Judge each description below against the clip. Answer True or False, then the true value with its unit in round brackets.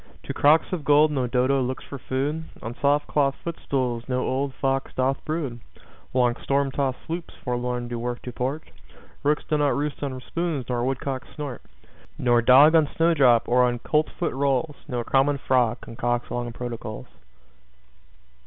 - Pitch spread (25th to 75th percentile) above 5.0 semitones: False (3.0 semitones)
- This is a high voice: False (135 Hz)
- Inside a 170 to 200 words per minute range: False (160 wpm)